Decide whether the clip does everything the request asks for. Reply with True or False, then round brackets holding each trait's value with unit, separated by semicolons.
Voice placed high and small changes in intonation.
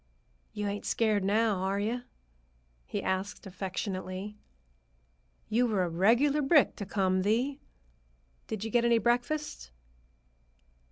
False (210 Hz; 3.8 semitones)